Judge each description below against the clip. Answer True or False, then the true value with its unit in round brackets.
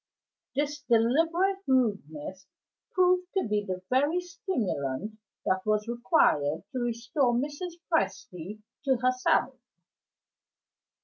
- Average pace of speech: False (100 wpm)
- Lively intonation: True (7.1 semitones)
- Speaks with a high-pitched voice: True (240 Hz)